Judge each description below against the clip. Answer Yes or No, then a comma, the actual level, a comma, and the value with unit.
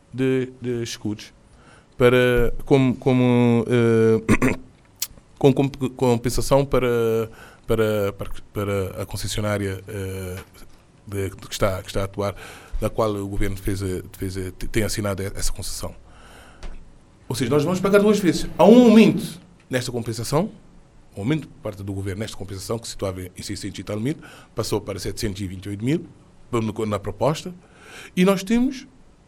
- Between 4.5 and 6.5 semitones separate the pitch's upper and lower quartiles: Yes, average, 5.2 semitones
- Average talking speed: Yes, average, 145 wpm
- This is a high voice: No, low, 115 Hz